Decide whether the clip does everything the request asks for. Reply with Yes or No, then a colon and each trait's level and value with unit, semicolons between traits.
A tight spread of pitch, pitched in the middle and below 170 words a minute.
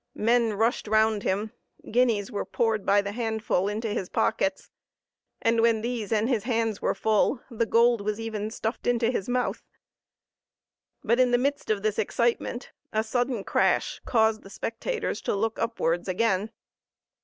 No: narrow, 2.1 semitones; high, 225 Hz; average, 160 wpm